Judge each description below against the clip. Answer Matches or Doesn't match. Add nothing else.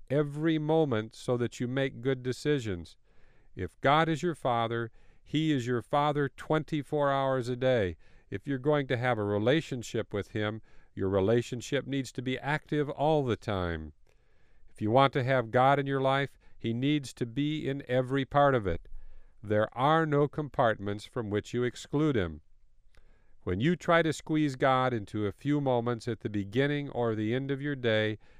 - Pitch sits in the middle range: Doesn't match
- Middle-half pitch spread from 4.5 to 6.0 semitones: Matches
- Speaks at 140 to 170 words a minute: Doesn't match